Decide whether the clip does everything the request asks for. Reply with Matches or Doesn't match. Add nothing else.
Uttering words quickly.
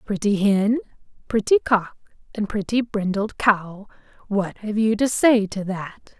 Doesn't match